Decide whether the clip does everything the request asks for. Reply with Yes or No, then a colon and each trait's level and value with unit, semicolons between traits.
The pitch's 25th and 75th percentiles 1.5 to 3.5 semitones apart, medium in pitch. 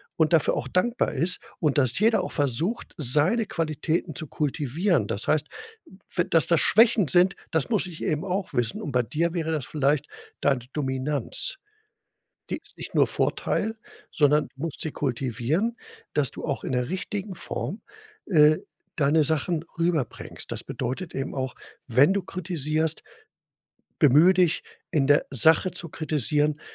No: average, 4.1 semitones; medium, 155 Hz